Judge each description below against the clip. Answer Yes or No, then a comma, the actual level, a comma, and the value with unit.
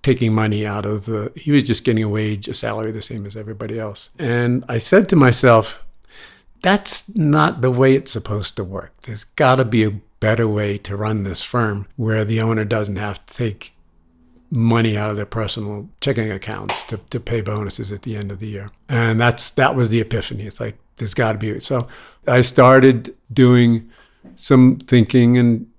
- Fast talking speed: No, average, 195 wpm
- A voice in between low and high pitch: No, low, 115 Hz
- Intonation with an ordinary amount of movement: Yes, average, 3.0 semitones